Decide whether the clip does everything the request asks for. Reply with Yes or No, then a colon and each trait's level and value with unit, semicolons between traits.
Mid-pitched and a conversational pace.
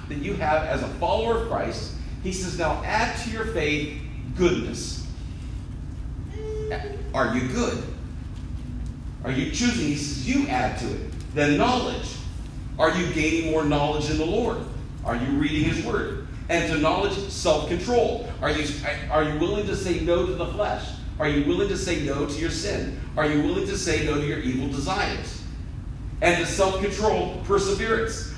Yes: medium, 150 Hz; average, 175 wpm